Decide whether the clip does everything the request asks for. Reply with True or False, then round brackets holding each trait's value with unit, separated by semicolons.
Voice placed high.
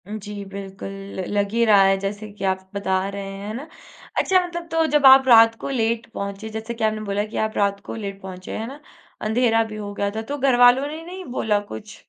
True (220 Hz)